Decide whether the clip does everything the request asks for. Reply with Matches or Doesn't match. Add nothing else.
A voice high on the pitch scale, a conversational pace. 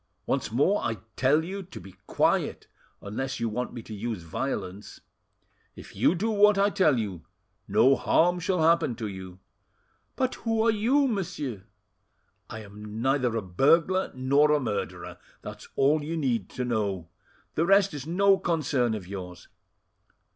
Doesn't match